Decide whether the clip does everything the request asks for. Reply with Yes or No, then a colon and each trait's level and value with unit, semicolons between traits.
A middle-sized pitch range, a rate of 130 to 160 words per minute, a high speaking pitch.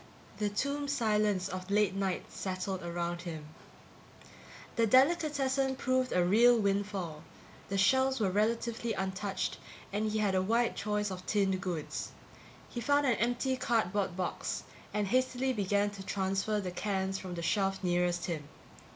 Yes: average, 4.0 semitones; average, 150 wpm; high, 205 Hz